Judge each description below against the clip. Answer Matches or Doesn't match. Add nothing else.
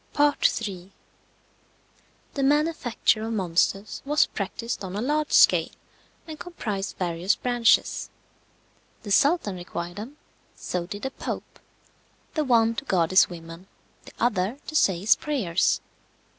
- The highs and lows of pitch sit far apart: Matches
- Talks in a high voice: Matches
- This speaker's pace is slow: Matches